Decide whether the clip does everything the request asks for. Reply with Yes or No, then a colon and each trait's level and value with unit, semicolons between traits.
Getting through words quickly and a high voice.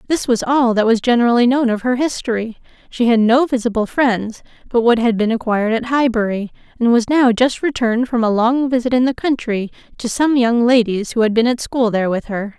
Yes: fast, 220 wpm; high, 235 Hz